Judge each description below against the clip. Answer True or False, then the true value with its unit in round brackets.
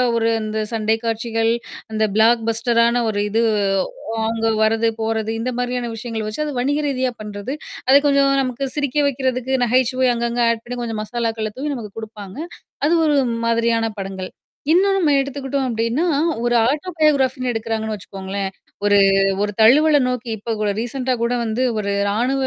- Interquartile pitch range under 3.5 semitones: True (2.9 semitones)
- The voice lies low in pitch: False (235 Hz)